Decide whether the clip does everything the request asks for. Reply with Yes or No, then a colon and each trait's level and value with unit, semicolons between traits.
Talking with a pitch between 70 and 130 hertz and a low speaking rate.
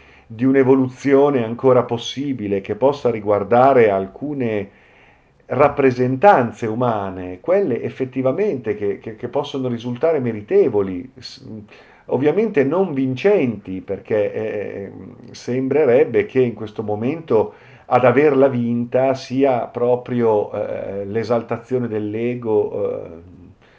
Yes: low, 125 Hz; slow, 95 wpm